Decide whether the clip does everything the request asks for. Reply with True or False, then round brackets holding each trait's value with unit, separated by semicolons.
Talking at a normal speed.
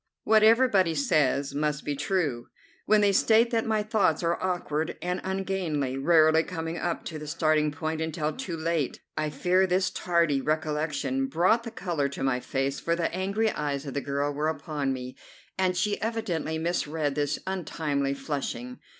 True (170 wpm)